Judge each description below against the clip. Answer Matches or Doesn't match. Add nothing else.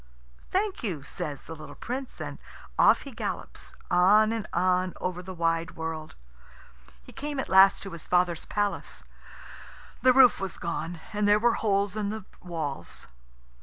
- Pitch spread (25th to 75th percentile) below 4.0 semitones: Doesn't match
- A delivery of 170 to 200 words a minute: Doesn't match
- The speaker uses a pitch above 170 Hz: Matches